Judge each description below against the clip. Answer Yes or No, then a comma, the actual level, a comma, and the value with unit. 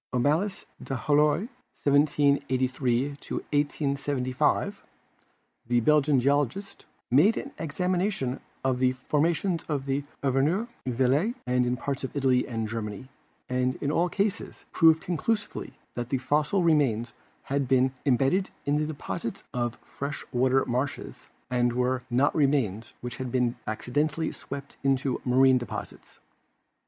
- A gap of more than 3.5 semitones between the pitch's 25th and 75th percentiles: No, average, 3.1 semitones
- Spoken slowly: Yes, slow, 125 wpm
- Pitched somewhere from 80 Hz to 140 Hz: Yes, low, 135 Hz